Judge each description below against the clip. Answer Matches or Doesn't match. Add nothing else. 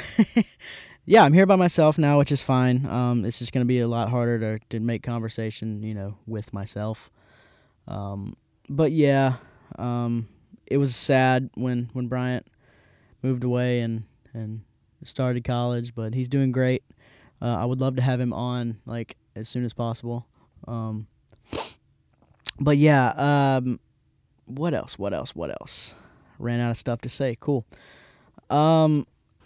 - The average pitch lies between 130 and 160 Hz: Doesn't match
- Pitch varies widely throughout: Doesn't match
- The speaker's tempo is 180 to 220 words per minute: Doesn't match